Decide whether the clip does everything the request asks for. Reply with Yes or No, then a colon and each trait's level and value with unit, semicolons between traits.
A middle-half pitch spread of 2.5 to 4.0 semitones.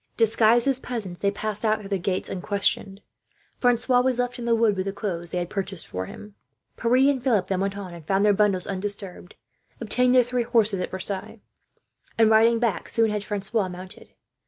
Yes: average, 3.3 semitones